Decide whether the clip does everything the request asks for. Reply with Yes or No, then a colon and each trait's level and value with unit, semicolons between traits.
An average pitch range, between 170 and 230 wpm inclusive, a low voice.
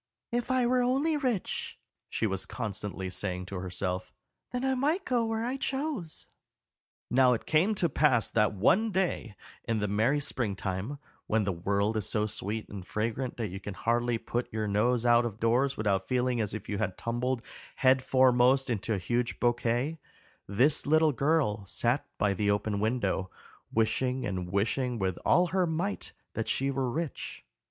No: wide, 6.5 semitones; average, 175 wpm; low, 120 Hz